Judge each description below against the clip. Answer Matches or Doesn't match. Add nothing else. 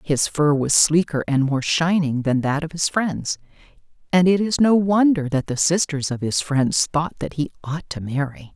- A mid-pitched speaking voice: Matches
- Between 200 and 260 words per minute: Matches